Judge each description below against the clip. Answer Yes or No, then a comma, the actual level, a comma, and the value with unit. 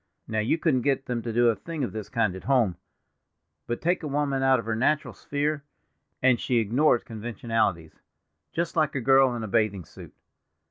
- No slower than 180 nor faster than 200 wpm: Yes, average, 195 wpm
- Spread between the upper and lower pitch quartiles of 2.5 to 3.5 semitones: No, average, 4.1 semitones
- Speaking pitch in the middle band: No, low, 120 Hz